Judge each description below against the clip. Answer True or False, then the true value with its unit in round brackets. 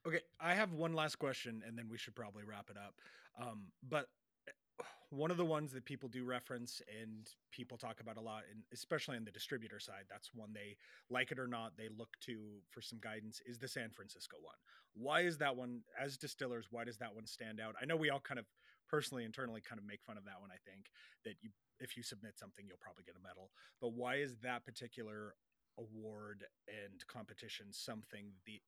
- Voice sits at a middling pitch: False (115 Hz)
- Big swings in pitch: False (3.2 semitones)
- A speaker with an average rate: False (220 wpm)